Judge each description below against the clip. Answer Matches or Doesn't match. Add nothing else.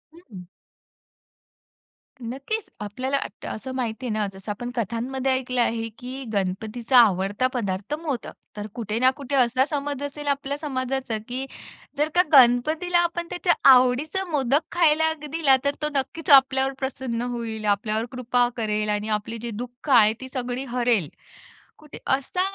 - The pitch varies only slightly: Doesn't match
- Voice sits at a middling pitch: Doesn't match